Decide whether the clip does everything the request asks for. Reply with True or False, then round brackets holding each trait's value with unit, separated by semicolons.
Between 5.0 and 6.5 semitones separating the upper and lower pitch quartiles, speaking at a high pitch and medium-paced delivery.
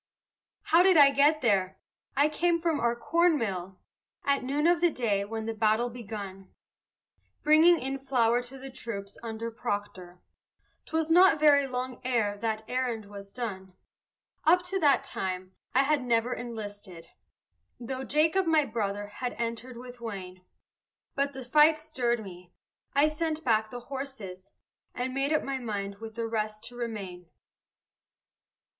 True (5.4 semitones; 240 Hz; 150 wpm)